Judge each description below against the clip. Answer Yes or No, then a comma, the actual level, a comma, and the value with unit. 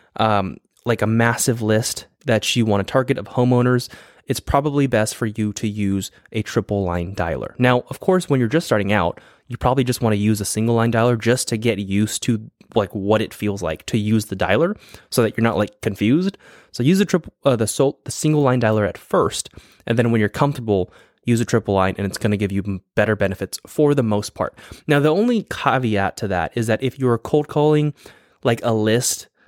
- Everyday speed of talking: No, fast, 225 wpm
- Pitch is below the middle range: Yes, low, 115 Hz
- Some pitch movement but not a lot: Yes, average, 3.8 semitones